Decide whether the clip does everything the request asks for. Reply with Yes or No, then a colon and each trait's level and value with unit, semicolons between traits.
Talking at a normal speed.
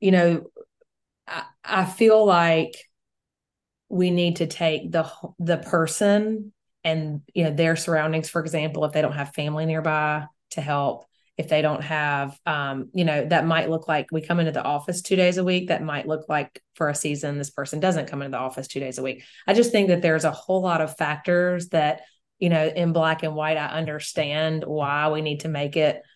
No: fast, 210 wpm